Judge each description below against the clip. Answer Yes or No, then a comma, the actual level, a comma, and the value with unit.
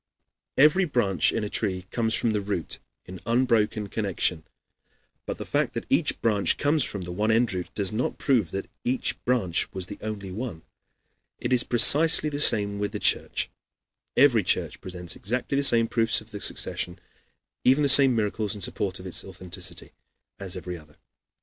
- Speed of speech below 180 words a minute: No, average, 185 wpm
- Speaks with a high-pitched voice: No, low, 105 Hz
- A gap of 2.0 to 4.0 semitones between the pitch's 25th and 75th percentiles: No, average, 4.7 semitones